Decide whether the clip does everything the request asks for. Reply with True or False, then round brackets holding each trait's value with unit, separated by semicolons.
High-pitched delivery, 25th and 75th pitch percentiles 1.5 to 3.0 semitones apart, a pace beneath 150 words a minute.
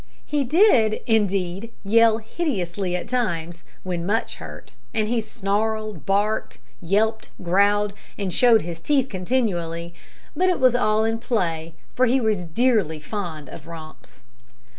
False (205 Hz; 4.8 semitones; 140 wpm)